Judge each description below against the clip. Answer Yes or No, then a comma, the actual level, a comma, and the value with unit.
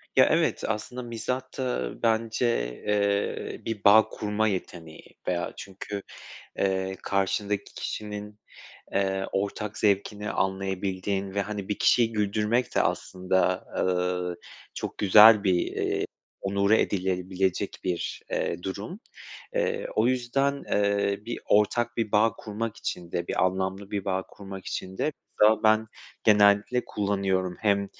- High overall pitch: No, low, 100 Hz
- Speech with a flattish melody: Yes, narrow, 2.3 semitones